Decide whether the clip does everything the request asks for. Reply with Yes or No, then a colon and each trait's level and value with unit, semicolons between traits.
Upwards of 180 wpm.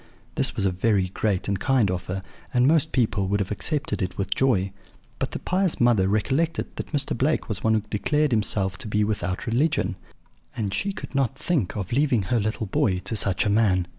Yes: fast, 205 wpm